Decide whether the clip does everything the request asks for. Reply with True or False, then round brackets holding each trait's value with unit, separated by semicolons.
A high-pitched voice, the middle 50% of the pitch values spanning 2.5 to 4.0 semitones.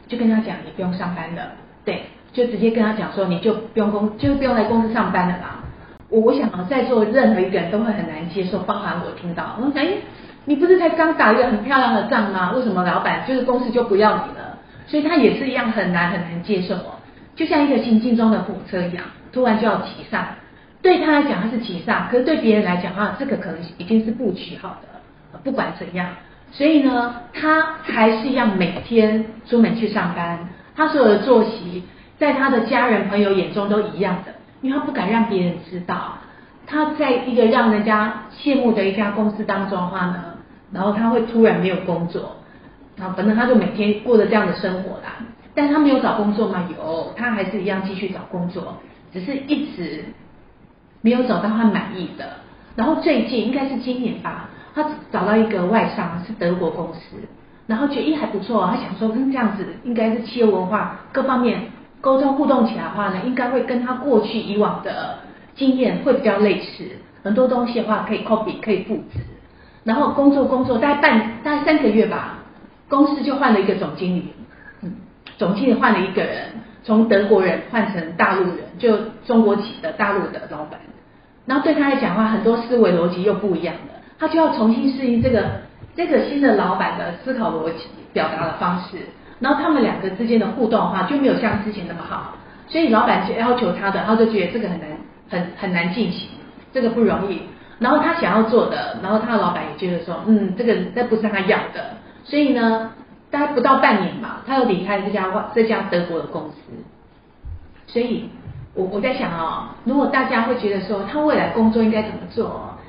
False (220 Hz; 4.4 semitones)